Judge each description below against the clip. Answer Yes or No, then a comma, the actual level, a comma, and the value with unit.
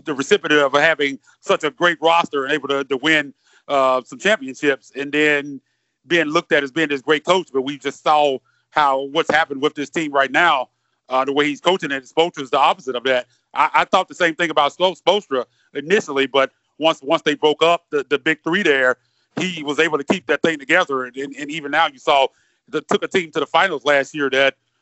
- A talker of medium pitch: Yes, medium, 145 Hz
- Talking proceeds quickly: Yes, fast, 230 wpm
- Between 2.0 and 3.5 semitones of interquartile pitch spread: Yes, average, 3.0 semitones